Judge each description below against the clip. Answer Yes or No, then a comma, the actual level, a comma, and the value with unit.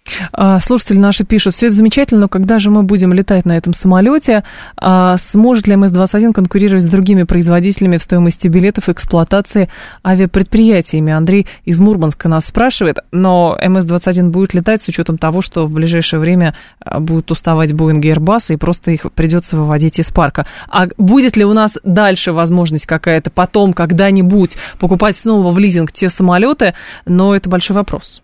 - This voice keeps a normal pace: No, fast, 165 wpm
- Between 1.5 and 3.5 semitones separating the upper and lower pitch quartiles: Yes, average, 3.1 semitones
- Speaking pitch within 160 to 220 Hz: Yes, medium, 185 Hz